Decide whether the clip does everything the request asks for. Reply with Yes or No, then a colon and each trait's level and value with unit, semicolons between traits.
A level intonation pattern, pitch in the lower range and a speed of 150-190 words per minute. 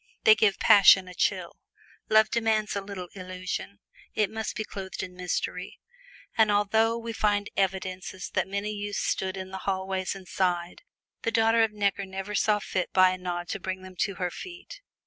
No: narrow, 2.3 semitones; high, 195 Hz; average, 185 wpm